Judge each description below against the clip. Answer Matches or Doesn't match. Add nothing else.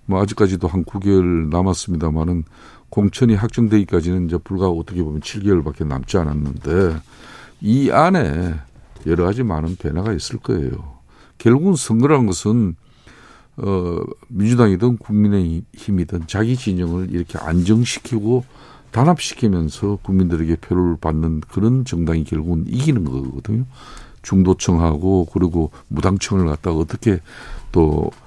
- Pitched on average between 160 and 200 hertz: Doesn't match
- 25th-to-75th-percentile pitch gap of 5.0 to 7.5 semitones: Doesn't match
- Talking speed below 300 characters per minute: Doesn't match